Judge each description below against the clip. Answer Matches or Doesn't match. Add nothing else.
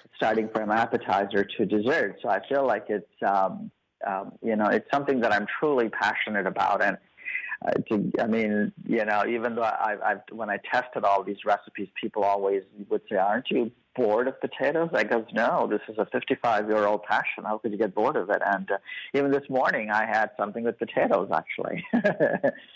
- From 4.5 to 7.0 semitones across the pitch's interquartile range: Doesn't match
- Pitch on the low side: Matches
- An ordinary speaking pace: Matches